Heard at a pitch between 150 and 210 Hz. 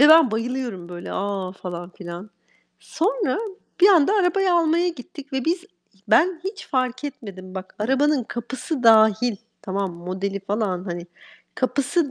No: high, 245 Hz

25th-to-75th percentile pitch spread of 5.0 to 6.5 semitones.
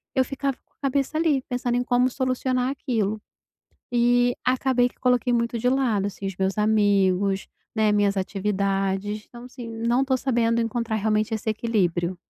No: average, 3.6 semitones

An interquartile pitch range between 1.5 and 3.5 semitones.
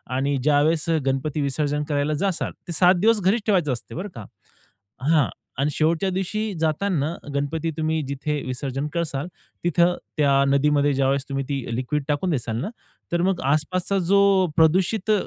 No: average, 3.9 semitones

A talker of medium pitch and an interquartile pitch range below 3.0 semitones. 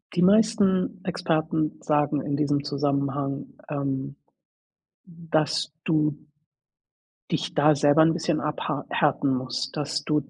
Yes: medium, 150 Hz; narrow, 2.4 semitones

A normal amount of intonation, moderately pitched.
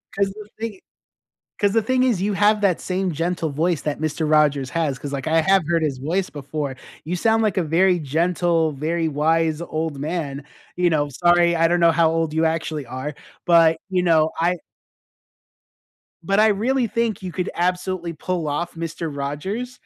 Yes: average, 3.3 semitones; medium, 165 Hz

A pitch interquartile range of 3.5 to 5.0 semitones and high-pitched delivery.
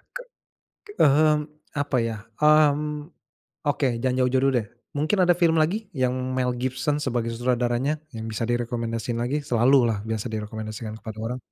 No: average, 4.1 semitones; low, 125 Hz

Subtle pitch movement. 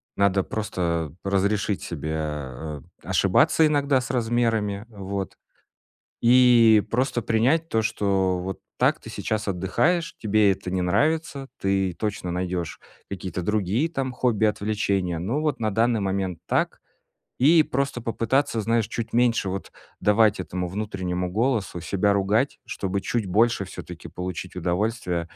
No: average, 4.1 semitones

